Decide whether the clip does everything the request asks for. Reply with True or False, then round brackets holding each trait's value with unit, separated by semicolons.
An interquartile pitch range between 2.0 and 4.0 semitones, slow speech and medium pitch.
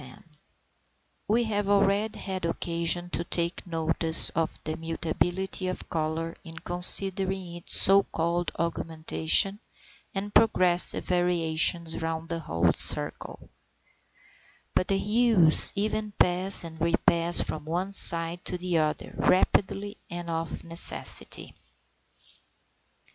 True (2.8 semitones; 115 wpm; 175 Hz)